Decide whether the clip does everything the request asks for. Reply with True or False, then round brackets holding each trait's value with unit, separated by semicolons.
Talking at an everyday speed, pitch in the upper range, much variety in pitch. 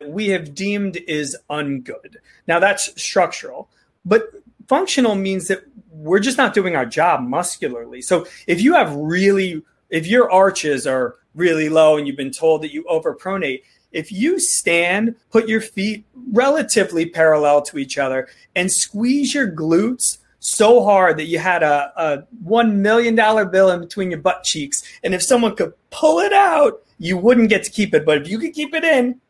True (180 wpm; 195 Hz; 6.6 semitones)